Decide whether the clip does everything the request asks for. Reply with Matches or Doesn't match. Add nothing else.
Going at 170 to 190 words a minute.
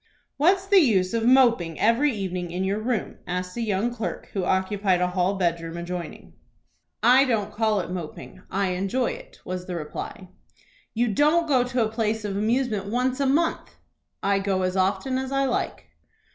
Matches